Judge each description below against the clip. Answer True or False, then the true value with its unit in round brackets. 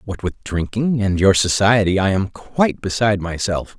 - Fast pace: False (175 wpm)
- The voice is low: True (100 Hz)